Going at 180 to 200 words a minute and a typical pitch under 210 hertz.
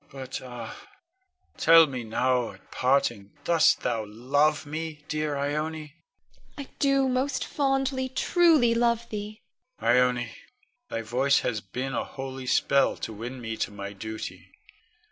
No: average, 145 wpm; medium, 140 Hz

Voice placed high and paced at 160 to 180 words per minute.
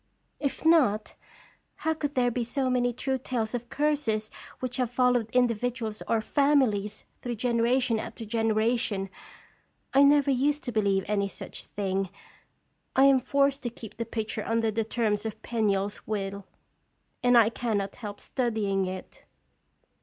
No: high, 230 Hz; average, 150 wpm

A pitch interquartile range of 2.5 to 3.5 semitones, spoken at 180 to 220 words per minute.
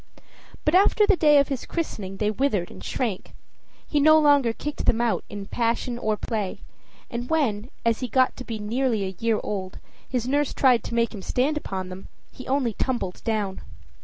No: average, 4.7 semitones; average, 195 wpm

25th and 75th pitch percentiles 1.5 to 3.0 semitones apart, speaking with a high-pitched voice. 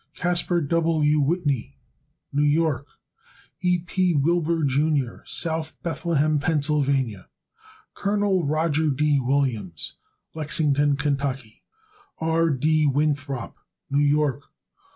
No: average, 2.7 semitones; medium, 150 Hz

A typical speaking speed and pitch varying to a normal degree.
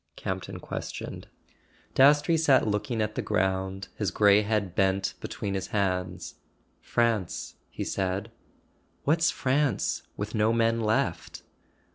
No: slow, 120 wpm; average, 3.3 semitones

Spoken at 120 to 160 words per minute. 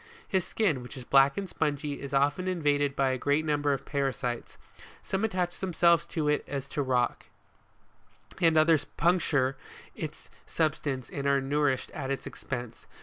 No: average, 175 wpm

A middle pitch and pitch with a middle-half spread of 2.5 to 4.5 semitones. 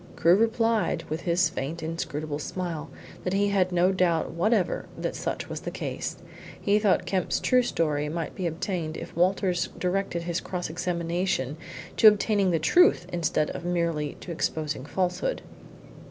Yes: medium, 175 Hz; average, 3.0 semitones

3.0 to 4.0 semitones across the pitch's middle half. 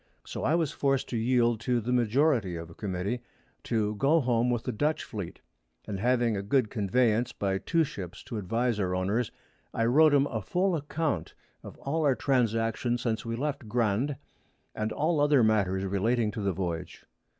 No: average, 4.6 semitones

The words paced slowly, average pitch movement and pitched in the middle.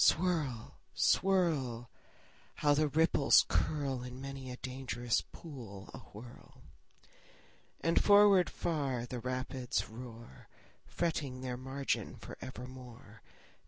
No: slow, 100 wpm; average, 3.7 semitones; low, 130 Hz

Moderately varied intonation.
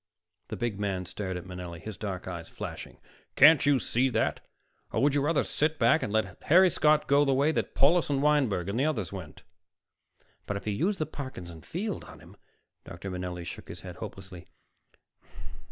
No: wide, 8.1 semitones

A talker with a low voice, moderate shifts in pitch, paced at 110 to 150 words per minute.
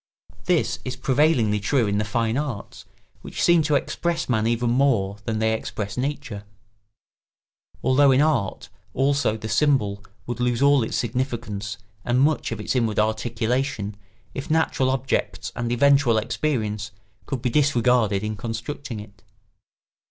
Yes: low, 120 Hz; average, 4.2 semitones; average, 145 wpm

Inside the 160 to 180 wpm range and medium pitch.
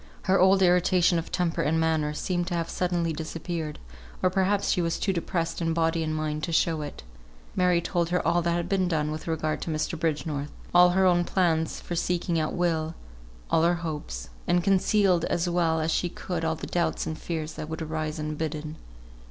No: average, 200 wpm; medium, 165 Hz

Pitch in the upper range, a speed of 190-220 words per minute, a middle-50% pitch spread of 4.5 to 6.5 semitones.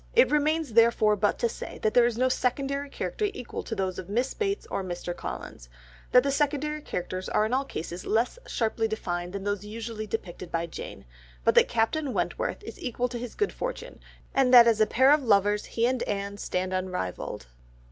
Yes: high, 230 Hz; average, 200 wpm; average, 5.2 semitones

